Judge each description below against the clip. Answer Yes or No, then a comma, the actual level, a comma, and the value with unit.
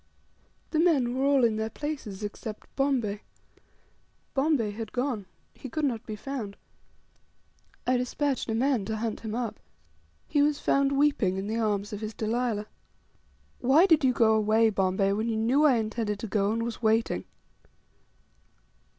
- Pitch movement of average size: Yes, average, 4.1 semitones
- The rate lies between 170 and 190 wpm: No, average, 160 wpm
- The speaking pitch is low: No, high, 230 Hz